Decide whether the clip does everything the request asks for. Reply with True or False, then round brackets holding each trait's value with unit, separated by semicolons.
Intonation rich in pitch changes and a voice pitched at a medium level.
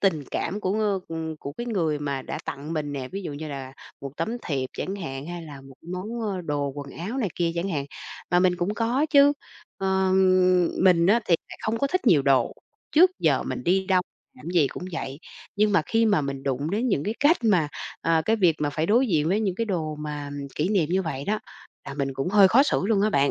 True (5.8 semitones; 175 Hz)